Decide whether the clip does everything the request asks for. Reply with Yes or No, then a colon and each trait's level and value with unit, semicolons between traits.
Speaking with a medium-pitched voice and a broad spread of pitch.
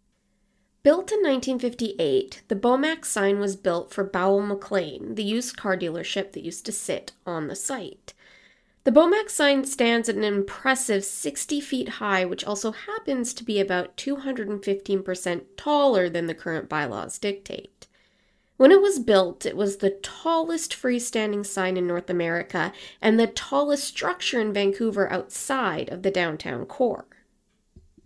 No: high, 205 Hz; wide, 6.2 semitones